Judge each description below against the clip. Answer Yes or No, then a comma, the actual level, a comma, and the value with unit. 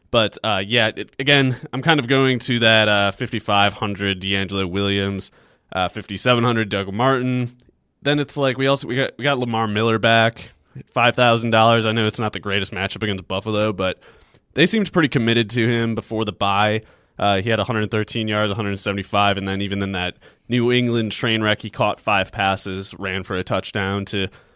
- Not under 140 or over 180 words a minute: No, average, 190 wpm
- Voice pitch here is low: Yes, low, 110 Hz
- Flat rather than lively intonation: No, average, 3.4 semitones